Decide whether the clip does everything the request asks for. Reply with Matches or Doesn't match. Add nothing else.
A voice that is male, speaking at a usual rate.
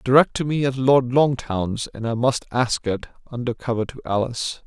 Matches